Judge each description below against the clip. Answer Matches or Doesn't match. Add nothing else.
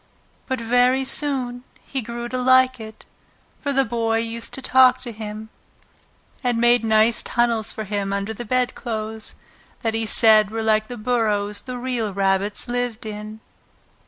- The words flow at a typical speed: Matches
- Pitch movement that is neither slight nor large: Doesn't match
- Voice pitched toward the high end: Matches